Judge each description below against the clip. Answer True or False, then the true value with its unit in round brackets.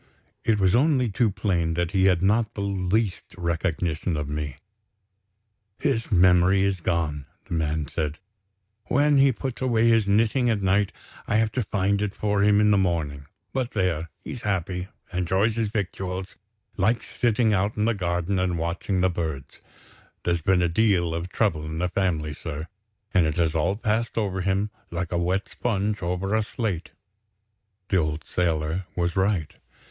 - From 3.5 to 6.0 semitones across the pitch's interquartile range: True (3.8 semitones)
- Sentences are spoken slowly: False (170 wpm)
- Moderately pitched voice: False (95 Hz)